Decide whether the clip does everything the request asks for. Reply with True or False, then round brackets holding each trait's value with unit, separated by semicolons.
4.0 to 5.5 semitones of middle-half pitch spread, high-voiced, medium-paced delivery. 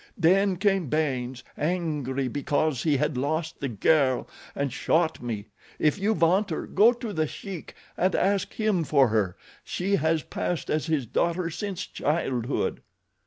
False (5.0 semitones; 160 Hz; 150 wpm)